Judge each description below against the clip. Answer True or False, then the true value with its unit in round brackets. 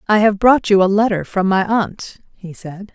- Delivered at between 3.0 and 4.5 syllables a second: True (4.4 syllables/s)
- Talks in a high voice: True (200 Hz)